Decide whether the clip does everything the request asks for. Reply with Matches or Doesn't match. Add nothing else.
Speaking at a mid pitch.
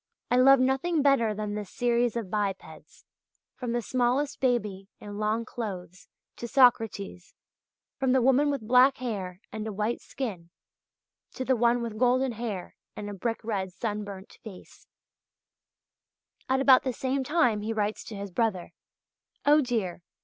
Doesn't match